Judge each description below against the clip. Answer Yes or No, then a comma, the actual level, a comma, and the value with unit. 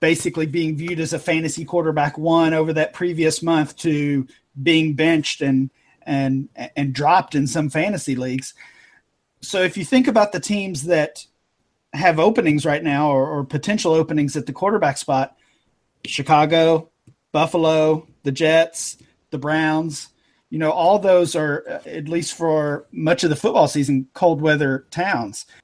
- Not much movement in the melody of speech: Yes, narrow, 2.3 semitones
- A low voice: No, medium, 155 Hz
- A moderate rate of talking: Yes, average, 150 wpm